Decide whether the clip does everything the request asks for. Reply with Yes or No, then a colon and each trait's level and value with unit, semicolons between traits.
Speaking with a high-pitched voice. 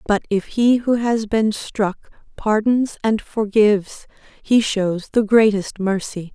Yes: high, 215 Hz